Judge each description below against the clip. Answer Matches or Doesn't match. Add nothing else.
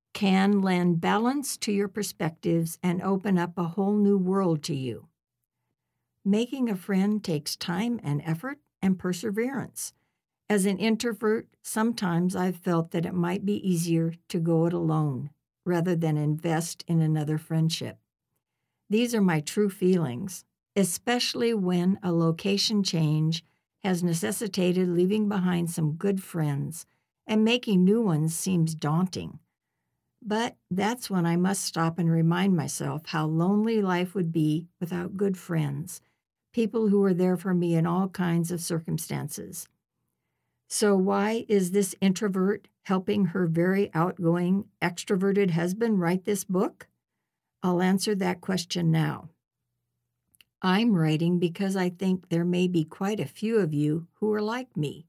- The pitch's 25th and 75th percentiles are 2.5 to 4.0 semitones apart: Matches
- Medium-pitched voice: Matches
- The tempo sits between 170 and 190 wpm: Doesn't match